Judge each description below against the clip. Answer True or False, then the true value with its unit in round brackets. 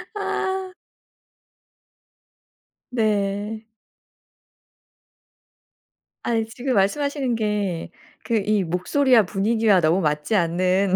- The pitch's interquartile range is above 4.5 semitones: False (3.9 semitones)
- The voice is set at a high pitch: True (210 Hz)